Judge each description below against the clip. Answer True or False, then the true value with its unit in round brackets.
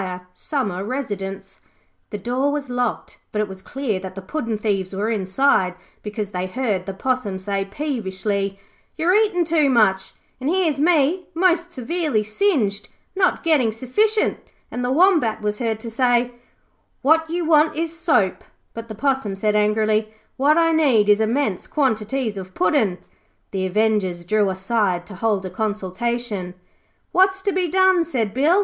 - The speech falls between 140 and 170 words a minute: True (155 wpm)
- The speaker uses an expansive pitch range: True (7.1 semitones)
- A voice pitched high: True (230 Hz)